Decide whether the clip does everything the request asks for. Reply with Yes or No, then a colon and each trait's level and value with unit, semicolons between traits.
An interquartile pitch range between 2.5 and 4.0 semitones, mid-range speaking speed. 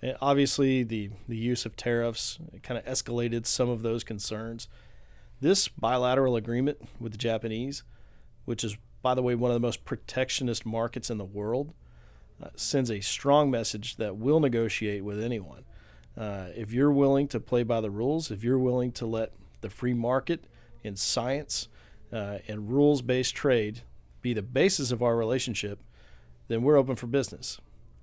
Yes: average, 3.1 semitones; average, 170 wpm